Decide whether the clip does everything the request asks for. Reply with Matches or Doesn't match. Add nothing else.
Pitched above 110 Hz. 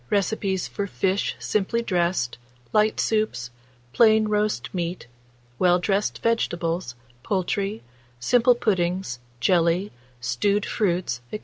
Matches